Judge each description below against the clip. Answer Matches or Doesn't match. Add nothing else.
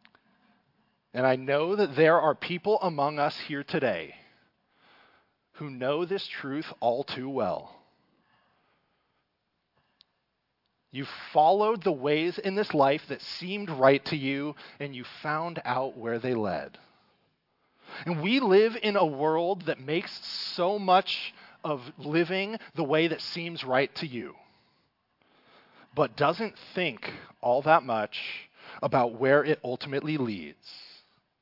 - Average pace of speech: Doesn't match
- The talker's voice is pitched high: Doesn't match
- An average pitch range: Matches